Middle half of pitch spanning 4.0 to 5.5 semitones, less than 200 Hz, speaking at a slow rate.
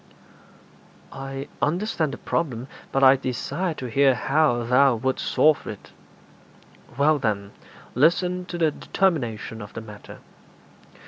Yes: average, 4.6 semitones; low, 135 Hz; slow, 125 wpm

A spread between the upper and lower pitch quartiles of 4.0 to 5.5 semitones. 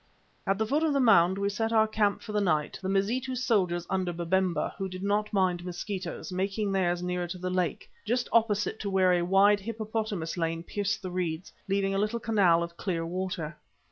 No: average, 3.0 semitones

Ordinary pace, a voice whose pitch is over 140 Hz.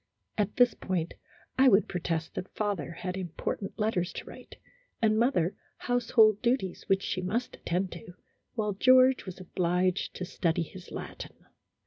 Yes: average, 150 wpm; high, 190 Hz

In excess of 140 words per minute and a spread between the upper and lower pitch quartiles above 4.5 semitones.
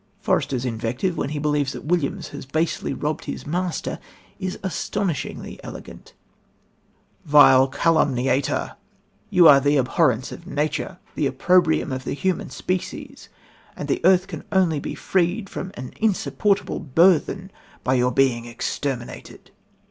No: slow, 135 wpm; wide, 5.4 semitones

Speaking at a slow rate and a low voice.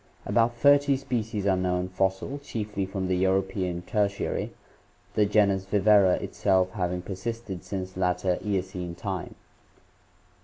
Yes: slow, 120 wpm; very low, 95 Hz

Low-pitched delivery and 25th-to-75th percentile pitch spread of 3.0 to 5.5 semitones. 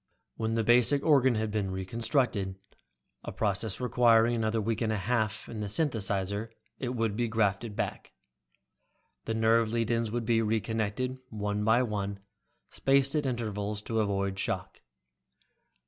No: low, 110 Hz; narrow, 2.4 semitones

